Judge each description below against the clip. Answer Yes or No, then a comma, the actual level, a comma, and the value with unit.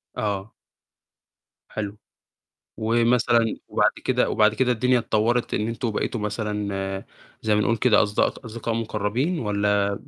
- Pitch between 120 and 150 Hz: No, low, 110 Hz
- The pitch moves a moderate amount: No, narrow, 2.0 semitones